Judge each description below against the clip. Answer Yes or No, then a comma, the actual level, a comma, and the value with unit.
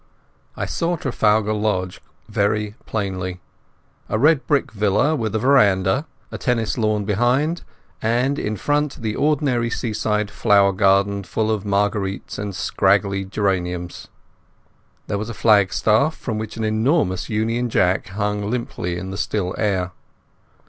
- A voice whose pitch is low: Yes, low, 105 Hz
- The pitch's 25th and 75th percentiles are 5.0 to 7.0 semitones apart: No, average, 3.2 semitones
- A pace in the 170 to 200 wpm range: No, slow, 135 wpm